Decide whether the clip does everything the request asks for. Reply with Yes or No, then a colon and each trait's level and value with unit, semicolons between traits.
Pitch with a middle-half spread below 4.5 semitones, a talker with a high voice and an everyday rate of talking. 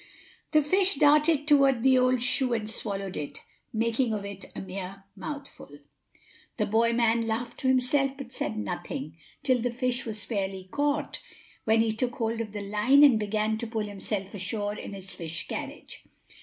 Yes: average, 4.1 semitones; high, 225 Hz; average, 175 wpm